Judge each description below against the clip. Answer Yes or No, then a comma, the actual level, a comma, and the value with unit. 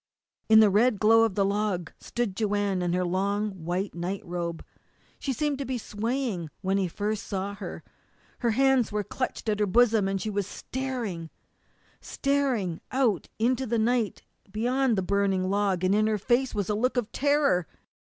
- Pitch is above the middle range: Yes, high, 210 Hz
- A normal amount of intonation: Yes, average, 4.1 semitones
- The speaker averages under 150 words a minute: No, average, 180 wpm